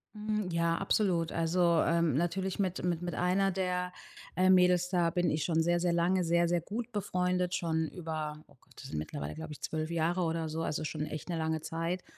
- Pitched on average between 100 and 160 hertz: No, medium, 170 Hz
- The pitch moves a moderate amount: No, narrow, 2.1 semitones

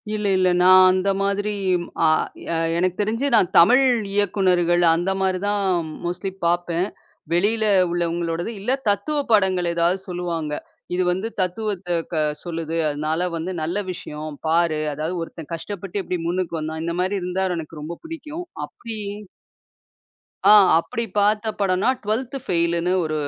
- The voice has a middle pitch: Yes, medium, 180 Hz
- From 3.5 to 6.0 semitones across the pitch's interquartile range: No, average, 3.1 semitones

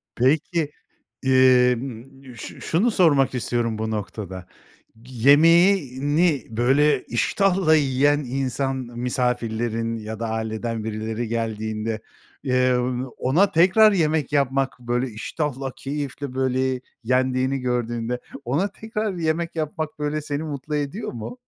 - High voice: No, low, 130 Hz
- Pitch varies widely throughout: No, average, 4.1 semitones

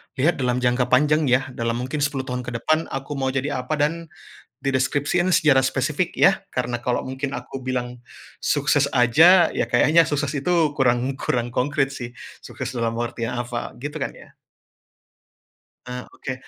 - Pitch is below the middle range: Yes, low, 130 Hz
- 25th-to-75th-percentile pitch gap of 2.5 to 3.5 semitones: Yes, average, 2.9 semitones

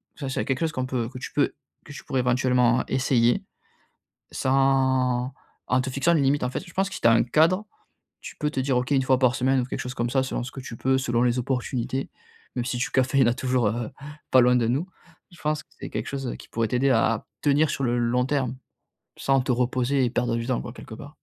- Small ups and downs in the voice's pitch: Yes, narrow, 1.8 semitones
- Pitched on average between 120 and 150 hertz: Yes, low, 130 Hz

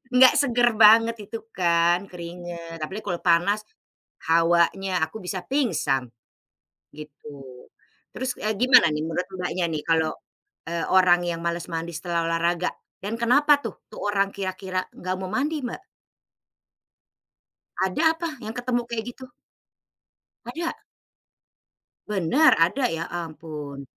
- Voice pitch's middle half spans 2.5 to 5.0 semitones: No, wide, 5.4 semitones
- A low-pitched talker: No, medium, 185 Hz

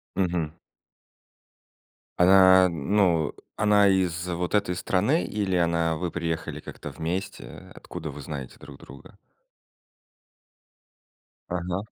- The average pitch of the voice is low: Yes, very low, 90 Hz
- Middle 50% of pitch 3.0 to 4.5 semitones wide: No, narrow, 2.5 semitones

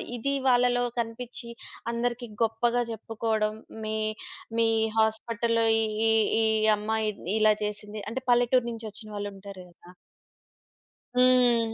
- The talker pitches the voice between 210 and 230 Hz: Yes, high, 225 Hz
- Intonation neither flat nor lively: No, narrow, 2.0 semitones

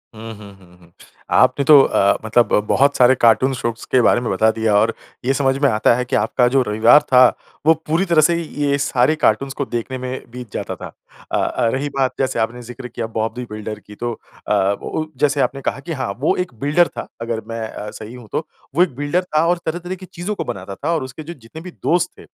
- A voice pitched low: Yes, low, 130 Hz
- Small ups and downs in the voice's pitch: No, average, 4.4 semitones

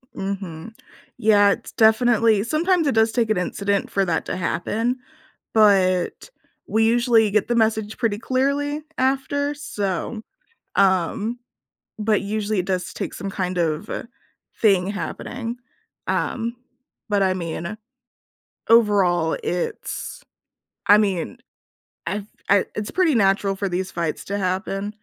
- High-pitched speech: Yes, high, 210 Hz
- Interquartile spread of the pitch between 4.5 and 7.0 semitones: No, average, 3.2 semitones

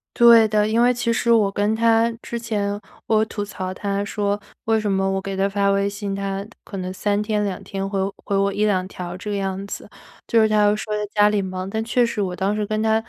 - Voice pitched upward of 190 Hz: Yes, high, 205 Hz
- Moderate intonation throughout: No, narrow, 1.8 semitones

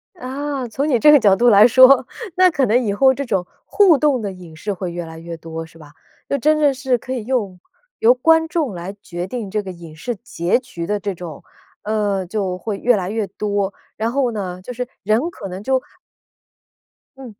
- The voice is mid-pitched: No, high, 215 Hz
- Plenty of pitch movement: Yes, wide, 6.0 semitones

